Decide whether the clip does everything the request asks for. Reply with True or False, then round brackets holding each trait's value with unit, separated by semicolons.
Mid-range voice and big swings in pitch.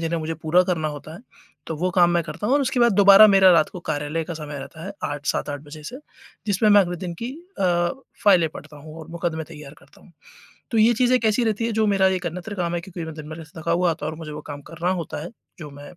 False (170 Hz; 4.1 semitones)